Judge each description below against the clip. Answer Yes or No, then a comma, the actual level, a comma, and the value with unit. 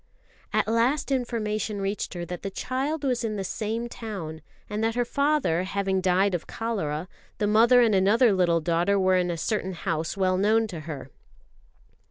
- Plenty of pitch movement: No, average, 4.3 semitones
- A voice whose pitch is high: Yes, high, 200 Hz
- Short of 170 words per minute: No, average, 180 wpm